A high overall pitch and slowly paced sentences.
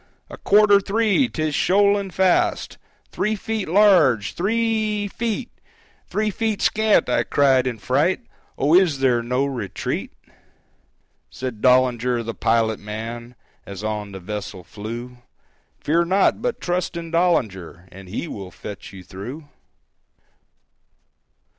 No: medium, 140 Hz; slow, 130 wpm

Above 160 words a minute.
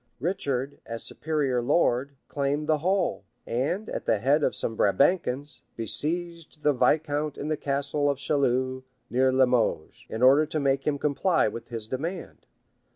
No: average, 155 wpm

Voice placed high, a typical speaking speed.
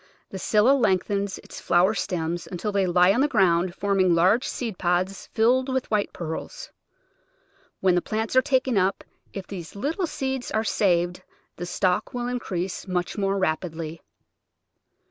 Yes: high, 195 Hz; average, 160 wpm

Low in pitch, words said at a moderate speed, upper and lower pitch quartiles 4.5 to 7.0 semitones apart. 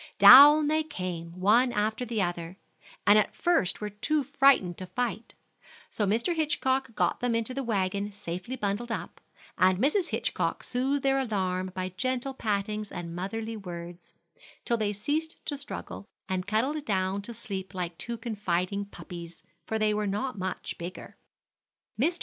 No: high, 210 Hz; average, 160 wpm; wide, 5.5 semitones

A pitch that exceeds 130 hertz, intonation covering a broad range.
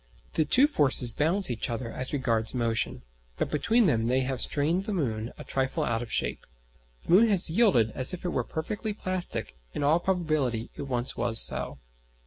Yes: medium, 140 Hz; wide, 7.1 semitones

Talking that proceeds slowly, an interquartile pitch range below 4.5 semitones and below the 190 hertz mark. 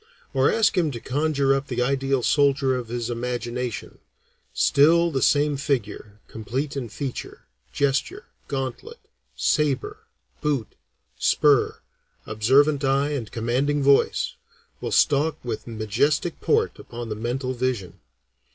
Yes: slow, 125 wpm; average, 3.2 semitones; low, 135 Hz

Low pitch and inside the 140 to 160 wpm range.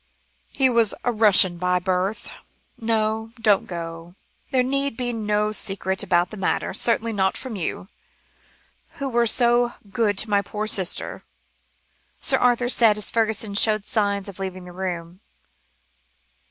No: high, 210 Hz; average, 145 wpm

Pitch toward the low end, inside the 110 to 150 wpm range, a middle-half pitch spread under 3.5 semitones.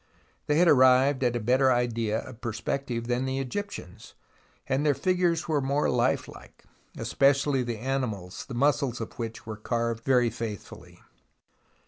Yes: low, 125 Hz; average, 145 wpm; average, 2.9 semitones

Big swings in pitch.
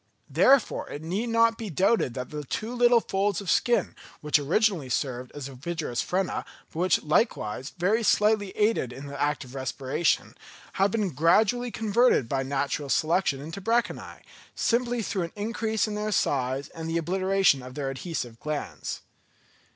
Yes: wide, 7.5 semitones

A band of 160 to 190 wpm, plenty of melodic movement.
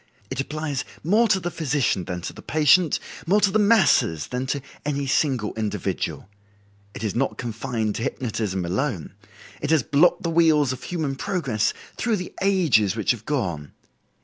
Yes: average, 170 wpm; wide, 7.0 semitones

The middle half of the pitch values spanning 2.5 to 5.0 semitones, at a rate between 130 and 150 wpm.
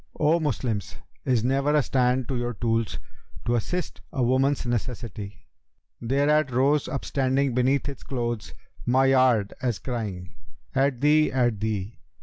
Yes: average, 2.8 semitones; average, 145 wpm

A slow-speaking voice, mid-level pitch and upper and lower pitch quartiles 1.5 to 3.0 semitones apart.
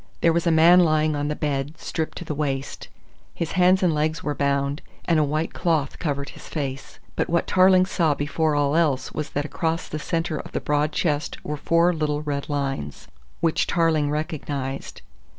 No: average, 195 wpm; medium, 155 Hz; narrow, 2.4 semitones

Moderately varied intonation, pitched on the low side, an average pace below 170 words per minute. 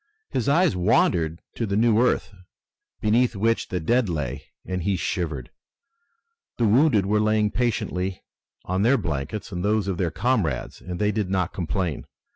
Yes: average, 4.0 semitones; low, 100 Hz; average, 160 wpm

